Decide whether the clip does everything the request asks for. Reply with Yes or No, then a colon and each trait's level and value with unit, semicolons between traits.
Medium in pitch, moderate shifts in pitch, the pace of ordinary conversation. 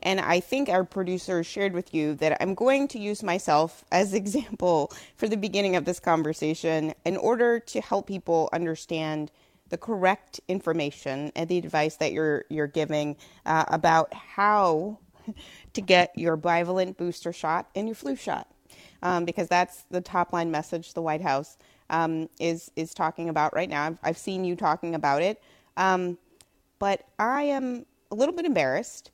Yes: medium, 175 Hz; average, 3.8 semitones; average, 170 wpm